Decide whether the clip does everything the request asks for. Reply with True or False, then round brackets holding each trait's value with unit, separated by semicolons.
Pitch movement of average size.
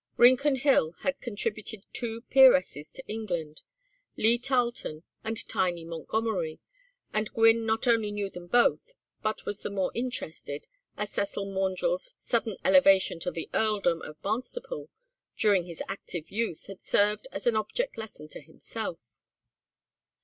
True (4.3 semitones)